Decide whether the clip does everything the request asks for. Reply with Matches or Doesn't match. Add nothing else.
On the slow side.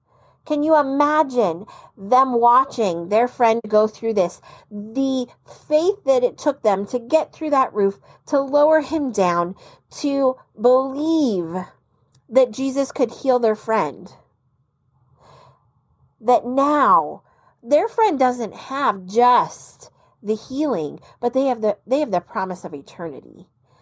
Matches